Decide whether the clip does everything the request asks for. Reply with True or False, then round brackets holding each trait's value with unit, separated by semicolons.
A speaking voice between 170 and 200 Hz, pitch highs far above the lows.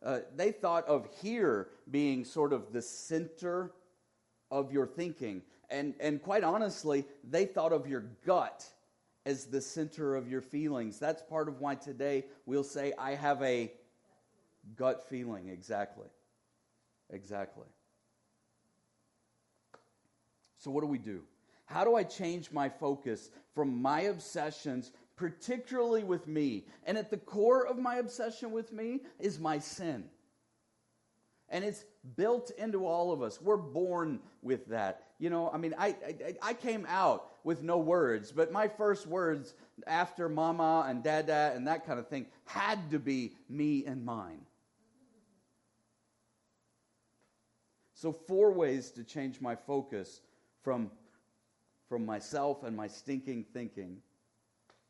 False (140 Hz; 6.3 semitones)